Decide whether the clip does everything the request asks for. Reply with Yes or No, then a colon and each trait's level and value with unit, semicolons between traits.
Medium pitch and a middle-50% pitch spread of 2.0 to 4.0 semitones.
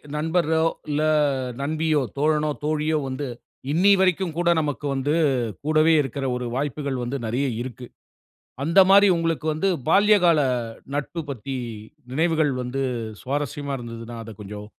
Yes: medium, 150 Hz; average, 3.3 semitones